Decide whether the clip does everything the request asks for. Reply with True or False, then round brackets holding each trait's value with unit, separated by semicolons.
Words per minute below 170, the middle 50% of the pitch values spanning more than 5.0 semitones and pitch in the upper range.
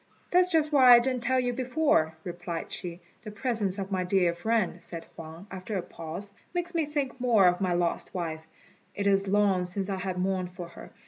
False (205 wpm; 5.6 semitones; 195 Hz)